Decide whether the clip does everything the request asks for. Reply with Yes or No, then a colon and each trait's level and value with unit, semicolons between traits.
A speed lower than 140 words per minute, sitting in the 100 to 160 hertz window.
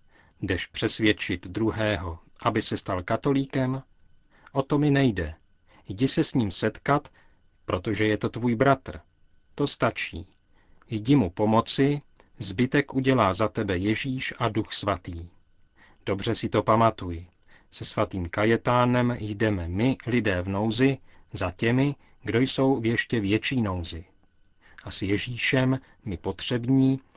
Yes: average, 130 wpm; low, 110 Hz